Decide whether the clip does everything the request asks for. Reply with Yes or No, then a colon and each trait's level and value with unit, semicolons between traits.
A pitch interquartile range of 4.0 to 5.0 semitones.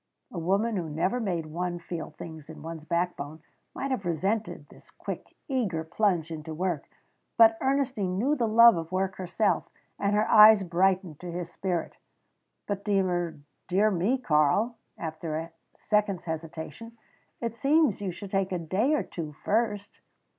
Yes: average, 4.6 semitones